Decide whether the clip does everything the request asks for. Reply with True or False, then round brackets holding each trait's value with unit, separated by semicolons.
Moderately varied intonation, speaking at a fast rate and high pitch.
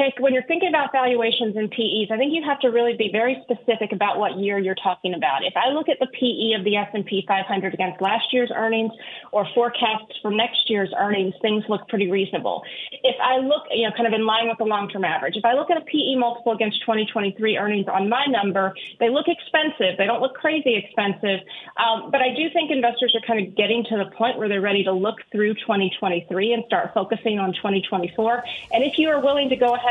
True (3.5 semitones; 225 wpm; 225 Hz)